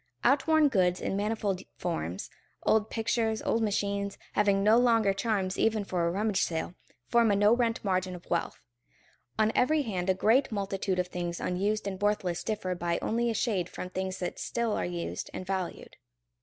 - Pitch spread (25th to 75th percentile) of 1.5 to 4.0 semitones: Yes, average, 3.4 semitones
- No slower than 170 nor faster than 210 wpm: Yes, average, 180 wpm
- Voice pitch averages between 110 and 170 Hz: No, high, 200 Hz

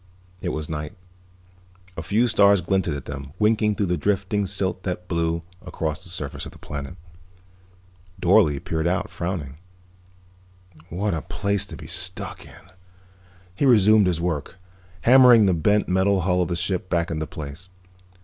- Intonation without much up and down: No, average, 3.7 semitones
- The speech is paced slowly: No, average, 160 wpm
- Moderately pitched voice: No, very low, 90 Hz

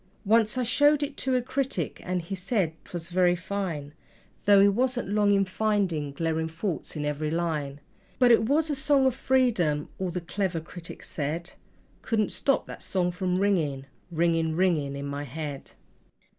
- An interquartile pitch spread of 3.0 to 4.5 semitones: No, average, 5.3 semitones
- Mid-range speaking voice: Yes, medium, 180 Hz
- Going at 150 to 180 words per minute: Yes, average, 170 wpm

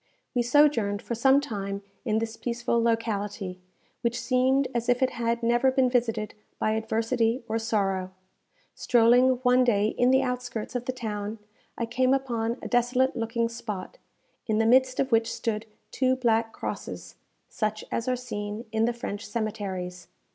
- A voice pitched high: Yes, high, 230 Hz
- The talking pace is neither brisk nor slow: Yes, average, 160 wpm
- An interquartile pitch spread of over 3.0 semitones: No, narrow, 2.5 semitones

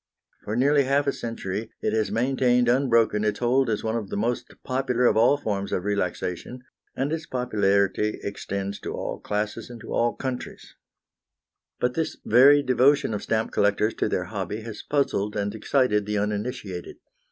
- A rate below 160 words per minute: No, average, 170 wpm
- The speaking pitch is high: No, low, 115 Hz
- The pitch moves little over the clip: No, average, 3.6 semitones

